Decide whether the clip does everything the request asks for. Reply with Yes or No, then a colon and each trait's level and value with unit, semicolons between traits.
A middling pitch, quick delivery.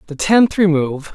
No: medium, 170 Hz; average, 155 wpm